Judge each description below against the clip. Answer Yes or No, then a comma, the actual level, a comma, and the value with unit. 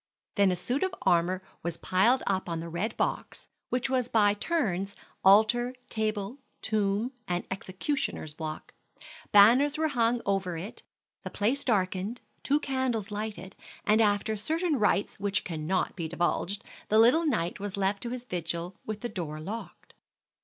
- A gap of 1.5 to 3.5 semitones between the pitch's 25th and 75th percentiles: No, average, 4.7 semitones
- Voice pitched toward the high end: Yes, high, 205 Hz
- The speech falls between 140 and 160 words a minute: Yes, average, 155 wpm